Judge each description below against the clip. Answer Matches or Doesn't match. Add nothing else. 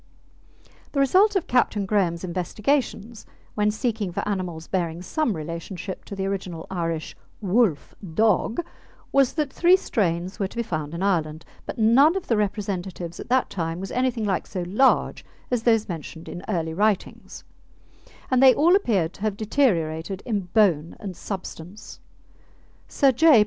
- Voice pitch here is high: Matches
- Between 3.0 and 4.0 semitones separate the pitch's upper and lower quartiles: Doesn't match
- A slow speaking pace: Doesn't match